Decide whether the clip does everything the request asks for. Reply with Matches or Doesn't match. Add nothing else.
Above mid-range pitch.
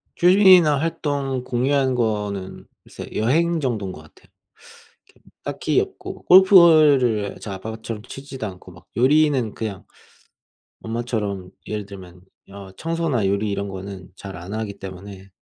Doesn't match